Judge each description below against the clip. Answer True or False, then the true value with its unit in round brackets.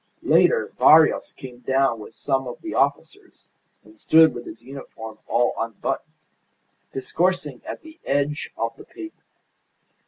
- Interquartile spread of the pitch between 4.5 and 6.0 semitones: True (5.1 semitones)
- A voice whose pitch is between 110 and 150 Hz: True (135 Hz)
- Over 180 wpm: False (135 wpm)